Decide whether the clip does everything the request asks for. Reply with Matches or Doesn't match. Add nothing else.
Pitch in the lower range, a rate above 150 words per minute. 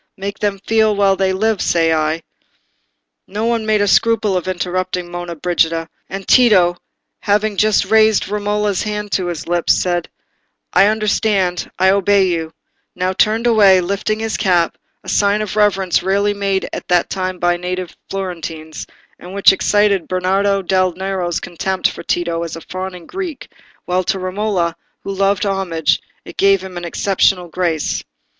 Doesn't match